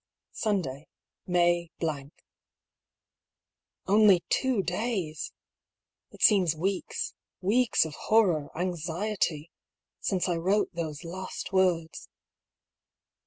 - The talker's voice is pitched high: No, medium, 180 Hz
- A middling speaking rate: No, slow, 100 wpm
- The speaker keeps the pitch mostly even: No, average, 3.5 semitones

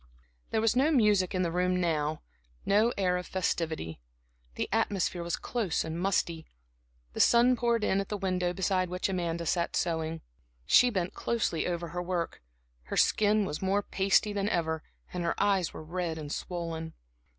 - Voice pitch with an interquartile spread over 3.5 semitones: No, average, 3.1 semitones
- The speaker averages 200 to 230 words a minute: No, average, 175 wpm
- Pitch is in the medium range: Yes, medium, 180 Hz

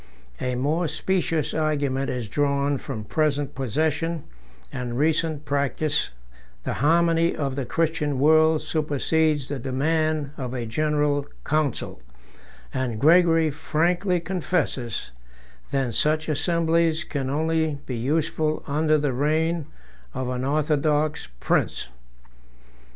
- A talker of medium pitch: Yes, medium, 150 Hz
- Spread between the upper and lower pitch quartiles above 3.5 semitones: No, average, 2.7 semitones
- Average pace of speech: No, slow, 110 wpm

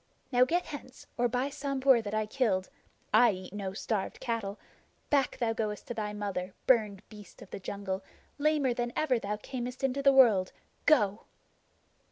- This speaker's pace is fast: No, average, 175 wpm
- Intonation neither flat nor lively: Yes, average, 4.4 semitones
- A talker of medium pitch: No, high, 230 Hz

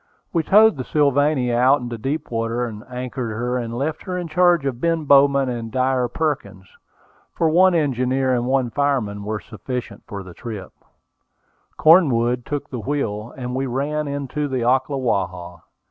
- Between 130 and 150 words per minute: No, average, 160 wpm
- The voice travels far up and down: No, average, 3.6 semitones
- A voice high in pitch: No, low, 130 Hz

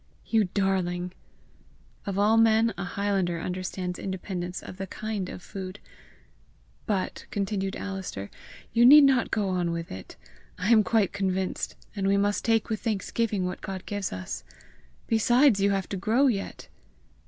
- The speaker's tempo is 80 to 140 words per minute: No, average, 155 wpm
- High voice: Yes, high, 195 Hz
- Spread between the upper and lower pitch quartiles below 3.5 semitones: Yes, average, 2.9 semitones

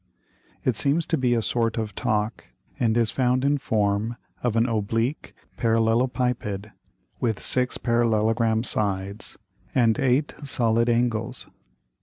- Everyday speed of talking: No, slow, 125 wpm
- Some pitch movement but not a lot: No, narrow, 2.2 semitones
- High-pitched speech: No, low, 115 Hz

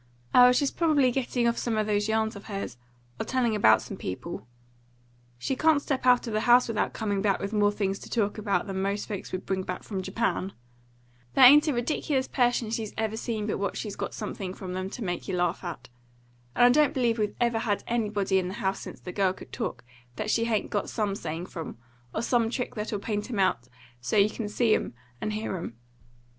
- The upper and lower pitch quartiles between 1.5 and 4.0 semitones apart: Yes, average, 3.5 semitones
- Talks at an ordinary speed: No, fast, 225 wpm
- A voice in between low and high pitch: No, high, 215 Hz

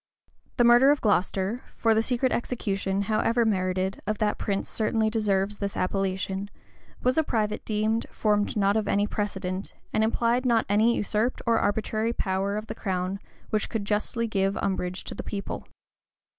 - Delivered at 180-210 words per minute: No, average, 160 wpm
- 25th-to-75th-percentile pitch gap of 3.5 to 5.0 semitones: No, narrow, 2.5 semitones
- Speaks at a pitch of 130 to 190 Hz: No, high, 210 Hz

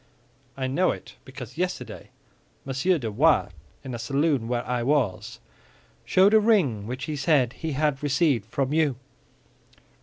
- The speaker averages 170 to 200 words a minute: No, average, 150 wpm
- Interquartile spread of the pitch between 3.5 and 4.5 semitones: Yes, average, 4.2 semitones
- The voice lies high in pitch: No, low, 135 Hz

